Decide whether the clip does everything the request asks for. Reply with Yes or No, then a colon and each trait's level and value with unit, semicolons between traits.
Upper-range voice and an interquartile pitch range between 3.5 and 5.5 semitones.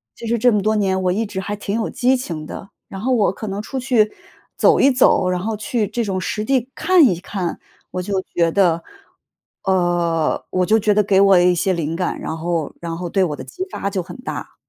Yes: high, 195 Hz; average, 3.8 semitones